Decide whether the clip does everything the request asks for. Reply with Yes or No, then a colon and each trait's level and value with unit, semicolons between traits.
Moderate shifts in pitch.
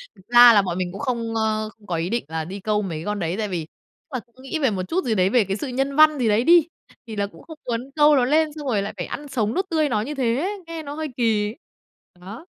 No: wide, 5.9 semitones